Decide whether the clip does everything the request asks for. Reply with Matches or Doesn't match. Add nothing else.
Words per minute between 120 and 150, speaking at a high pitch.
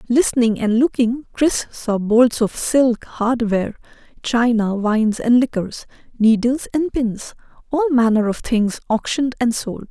Matches